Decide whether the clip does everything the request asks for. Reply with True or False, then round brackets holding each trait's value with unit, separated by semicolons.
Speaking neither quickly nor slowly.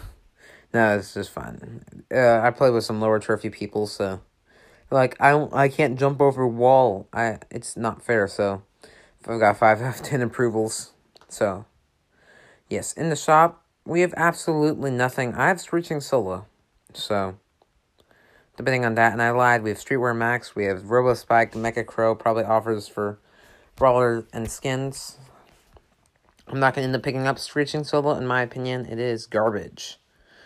True (165 wpm)